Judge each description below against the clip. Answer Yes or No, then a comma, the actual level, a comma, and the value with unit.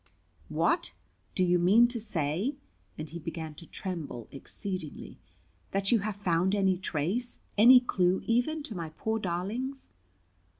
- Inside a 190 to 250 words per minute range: No, average, 140 wpm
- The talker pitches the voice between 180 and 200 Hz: Yes, high, 190 Hz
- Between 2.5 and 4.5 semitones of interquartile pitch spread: No, average, 5.0 semitones